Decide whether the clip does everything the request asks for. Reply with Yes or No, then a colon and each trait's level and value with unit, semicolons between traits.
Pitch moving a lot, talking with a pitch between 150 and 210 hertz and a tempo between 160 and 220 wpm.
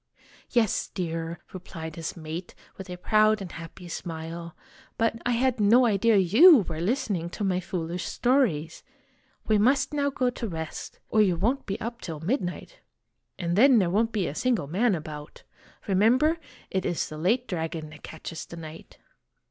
Yes: wide, 5.7 semitones; high, 190 Hz; average, 170 wpm